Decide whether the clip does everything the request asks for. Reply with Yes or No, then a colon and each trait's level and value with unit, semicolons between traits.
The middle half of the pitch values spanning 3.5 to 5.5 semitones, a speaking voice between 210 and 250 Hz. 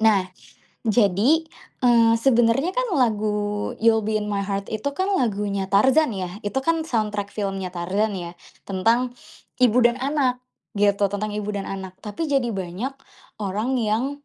Yes: average, 3.9 semitones; high, 215 Hz